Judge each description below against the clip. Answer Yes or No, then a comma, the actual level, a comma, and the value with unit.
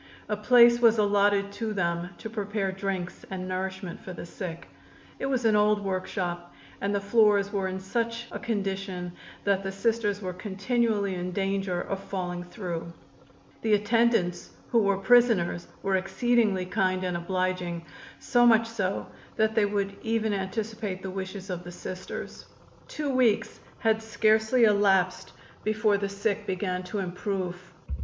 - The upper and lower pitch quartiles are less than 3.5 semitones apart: Yes, average, 2.9 semitones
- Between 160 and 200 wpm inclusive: No, average, 150 wpm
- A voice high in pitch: Yes, high, 200 Hz